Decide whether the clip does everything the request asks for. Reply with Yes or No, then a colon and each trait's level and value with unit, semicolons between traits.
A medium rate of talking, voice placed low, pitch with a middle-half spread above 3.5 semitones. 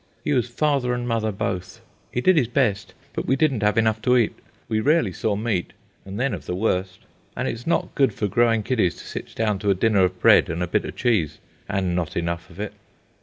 No: fast, 235 wpm; low, 110 Hz; average, 4.5 semitones